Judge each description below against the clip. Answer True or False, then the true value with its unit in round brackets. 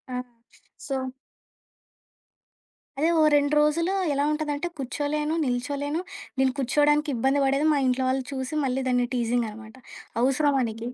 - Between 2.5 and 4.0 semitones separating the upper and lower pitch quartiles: True (2.9 semitones)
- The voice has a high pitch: True (275 Hz)